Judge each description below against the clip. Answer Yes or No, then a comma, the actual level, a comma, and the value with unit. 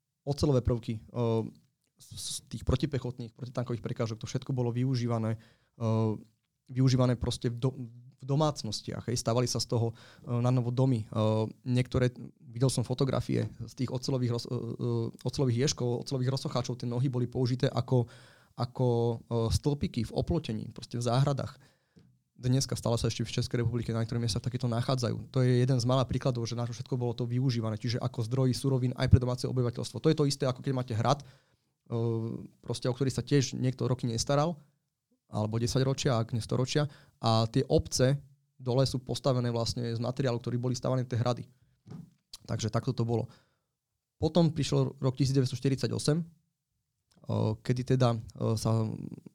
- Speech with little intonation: Yes, narrow, 2.3 semitones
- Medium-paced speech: Yes, average, 155 wpm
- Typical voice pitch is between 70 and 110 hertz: No, low, 125 Hz